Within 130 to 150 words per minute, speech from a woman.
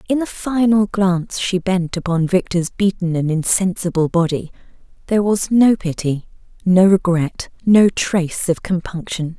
Yes: average, 140 wpm; female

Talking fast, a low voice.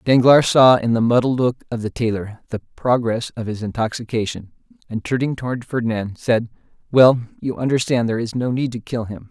No: average, 185 wpm; low, 120 Hz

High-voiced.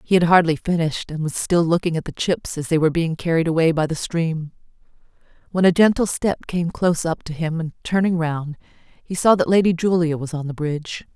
No: medium, 165 Hz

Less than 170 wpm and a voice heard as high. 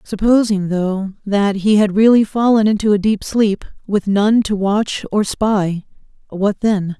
Yes: average, 155 wpm; high, 205 Hz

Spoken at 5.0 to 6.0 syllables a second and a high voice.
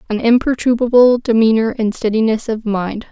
Yes: 5.2 syllables/s; high, 225 Hz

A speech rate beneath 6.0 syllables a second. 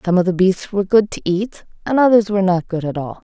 No: 6.1 syllables/s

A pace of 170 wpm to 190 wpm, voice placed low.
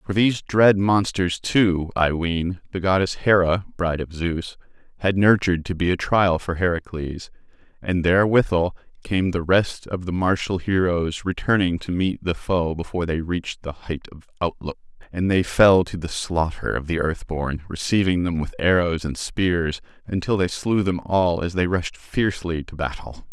Yes: average, 175 wpm; very low, 90 Hz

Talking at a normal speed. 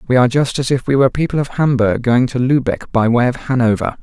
No: fast, 255 wpm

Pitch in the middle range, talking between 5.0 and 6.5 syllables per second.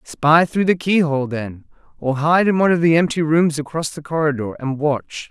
Yes: medium, 160 Hz; 5.2 syllables/s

